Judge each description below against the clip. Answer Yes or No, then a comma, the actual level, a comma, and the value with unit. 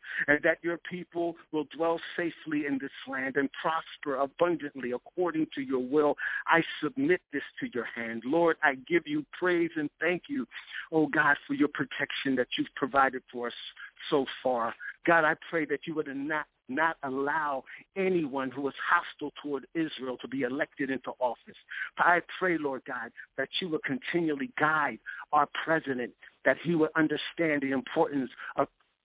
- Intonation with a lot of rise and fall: No, average, 3.4 semitones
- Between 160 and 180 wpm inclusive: Yes, average, 170 wpm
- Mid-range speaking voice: Yes, medium, 150 Hz